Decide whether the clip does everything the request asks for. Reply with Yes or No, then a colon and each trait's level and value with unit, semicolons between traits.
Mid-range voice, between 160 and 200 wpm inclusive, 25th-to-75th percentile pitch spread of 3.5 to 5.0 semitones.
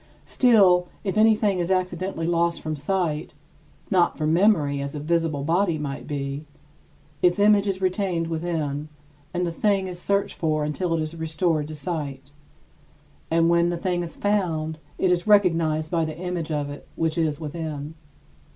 No: medium, 165 Hz; average, 165 wpm; average, 3.0 semitones